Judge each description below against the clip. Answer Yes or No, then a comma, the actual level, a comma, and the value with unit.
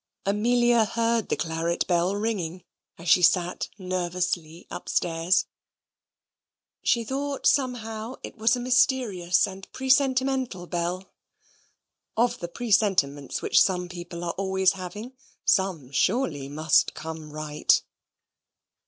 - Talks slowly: Yes, slow, 110 wpm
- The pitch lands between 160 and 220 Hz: Yes, medium, 185 Hz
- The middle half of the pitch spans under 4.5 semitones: No, average, 5.1 semitones